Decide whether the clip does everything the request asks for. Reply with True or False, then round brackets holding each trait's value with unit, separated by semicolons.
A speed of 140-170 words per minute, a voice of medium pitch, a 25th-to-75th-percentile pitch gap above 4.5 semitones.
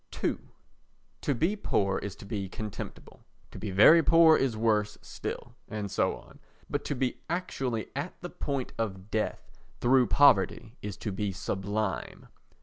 False (155 wpm; 110 Hz; 5.3 semitones)